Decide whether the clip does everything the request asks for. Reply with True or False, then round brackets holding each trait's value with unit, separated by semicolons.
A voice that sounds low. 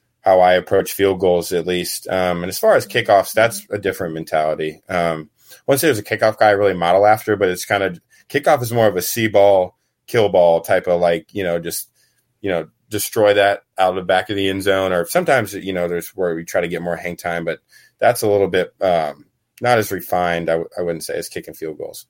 True (90 Hz)